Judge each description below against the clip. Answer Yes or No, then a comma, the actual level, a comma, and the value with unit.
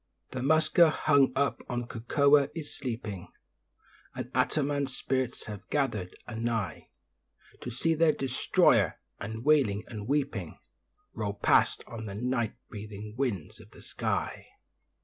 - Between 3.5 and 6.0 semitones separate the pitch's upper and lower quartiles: Yes, average, 4.8 semitones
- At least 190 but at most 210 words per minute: No, slow, 135 wpm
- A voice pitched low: Yes, low, 125 Hz